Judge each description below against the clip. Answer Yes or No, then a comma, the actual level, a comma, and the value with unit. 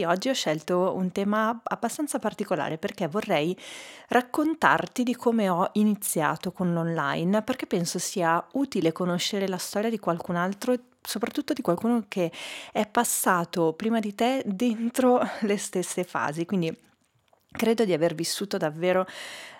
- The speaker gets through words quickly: No, average, 140 wpm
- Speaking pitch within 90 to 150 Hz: No, high, 200 Hz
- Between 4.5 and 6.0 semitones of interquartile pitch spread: Yes, average, 5.1 semitones